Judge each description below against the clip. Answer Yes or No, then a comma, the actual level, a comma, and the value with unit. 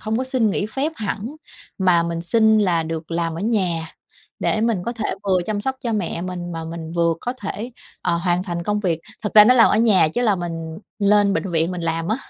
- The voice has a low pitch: No, high, 190 Hz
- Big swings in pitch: No, average, 4.5 semitones